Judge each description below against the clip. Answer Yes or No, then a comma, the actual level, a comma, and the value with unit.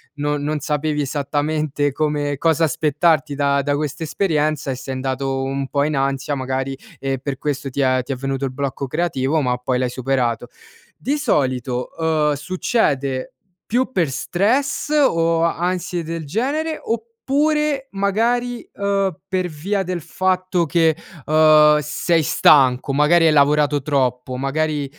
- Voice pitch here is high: No, medium, 150 Hz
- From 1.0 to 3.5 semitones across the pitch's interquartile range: No, average, 4.3 semitones